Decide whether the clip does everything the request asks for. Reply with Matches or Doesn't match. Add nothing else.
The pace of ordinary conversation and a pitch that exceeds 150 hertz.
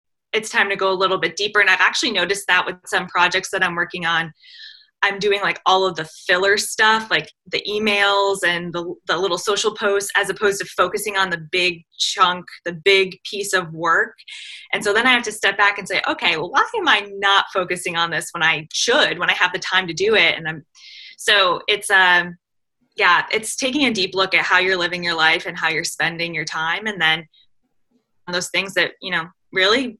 Doesn't match